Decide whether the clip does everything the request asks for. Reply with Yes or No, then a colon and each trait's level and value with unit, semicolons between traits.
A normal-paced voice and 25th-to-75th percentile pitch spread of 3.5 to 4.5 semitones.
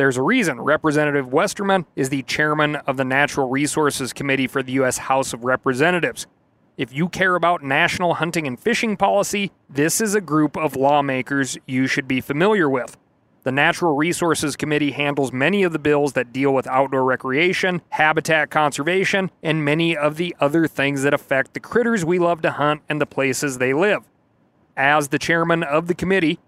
Yes: average, 180 wpm; average, 4.0 semitones